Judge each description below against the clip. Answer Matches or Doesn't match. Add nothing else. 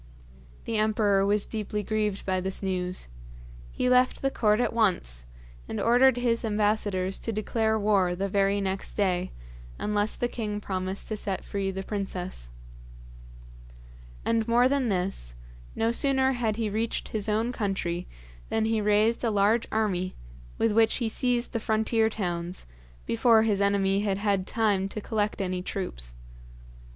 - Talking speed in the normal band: Matches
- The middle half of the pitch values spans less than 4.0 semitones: Matches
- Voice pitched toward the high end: Matches